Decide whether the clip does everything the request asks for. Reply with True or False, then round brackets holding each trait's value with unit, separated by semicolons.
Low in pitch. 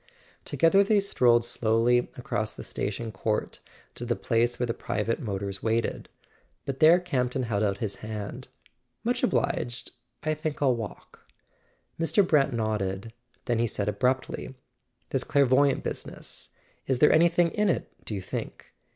True (120 Hz)